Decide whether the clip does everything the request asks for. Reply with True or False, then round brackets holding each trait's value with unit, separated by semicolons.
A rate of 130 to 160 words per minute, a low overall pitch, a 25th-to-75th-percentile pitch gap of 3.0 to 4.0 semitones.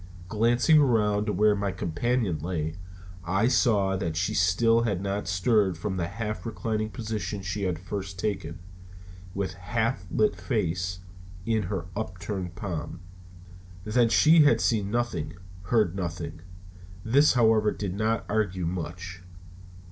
True (135 wpm; 100 Hz; 3.7 semitones)